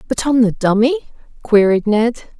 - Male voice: No, female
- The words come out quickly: No, average, 150 wpm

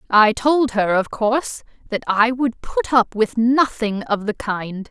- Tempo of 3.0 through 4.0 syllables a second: Yes, 3.9 syllables/s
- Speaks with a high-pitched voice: Yes, high, 225 Hz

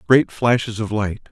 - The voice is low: Yes, low, 110 Hz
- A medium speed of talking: Yes, average, 180 wpm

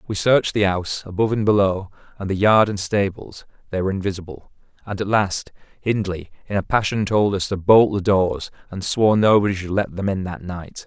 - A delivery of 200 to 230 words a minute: Yes, fast, 205 wpm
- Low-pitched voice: Yes, low, 100 Hz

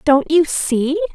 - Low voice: No, very high, 315 Hz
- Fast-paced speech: No, average, 155 wpm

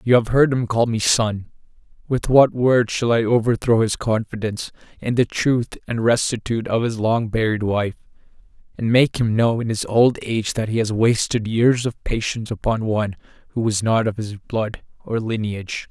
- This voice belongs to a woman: No, male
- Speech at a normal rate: Yes, average, 190 wpm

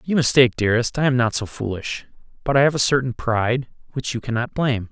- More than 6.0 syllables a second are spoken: Yes, 6.4 syllables/s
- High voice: No, low, 125 Hz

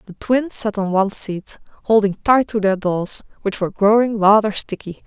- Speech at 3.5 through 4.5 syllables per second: No, 5.0 syllables/s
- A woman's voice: Yes, female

